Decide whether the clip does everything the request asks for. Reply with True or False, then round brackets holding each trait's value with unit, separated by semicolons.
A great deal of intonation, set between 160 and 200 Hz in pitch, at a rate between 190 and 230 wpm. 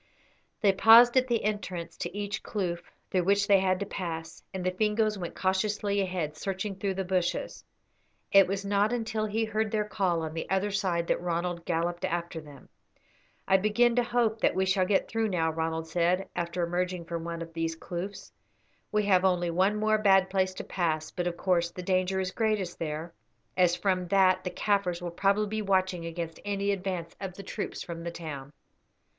False (2.9 semitones; 185 Hz; 195 wpm)